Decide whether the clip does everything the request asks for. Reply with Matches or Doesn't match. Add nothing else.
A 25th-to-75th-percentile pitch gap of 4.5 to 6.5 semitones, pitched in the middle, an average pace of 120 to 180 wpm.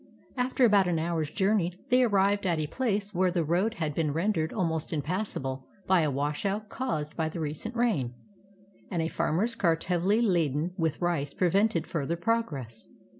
Matches